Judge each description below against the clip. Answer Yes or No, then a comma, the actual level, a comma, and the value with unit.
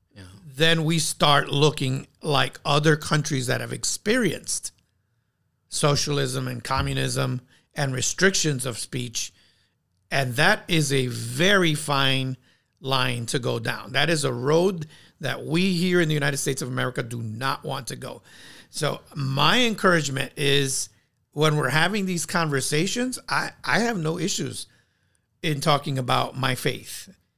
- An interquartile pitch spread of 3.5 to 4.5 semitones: Yes, average, 3.8 semitones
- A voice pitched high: No, medium, 140 Hz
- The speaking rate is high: No, average, 140 wpm